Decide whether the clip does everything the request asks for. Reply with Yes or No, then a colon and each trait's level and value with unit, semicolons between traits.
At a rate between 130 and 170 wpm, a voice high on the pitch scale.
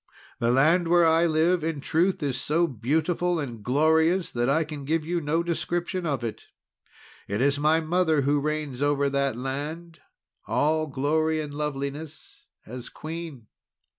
No: average, 155 wpm; medium, 155 Hz